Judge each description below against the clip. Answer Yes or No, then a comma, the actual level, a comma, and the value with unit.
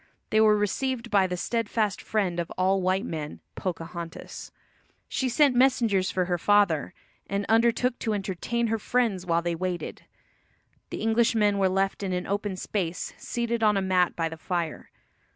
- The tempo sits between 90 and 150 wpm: No, average, 165 wpm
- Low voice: No, high, 200 Hz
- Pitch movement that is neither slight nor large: Yes, average, 3.8 semitones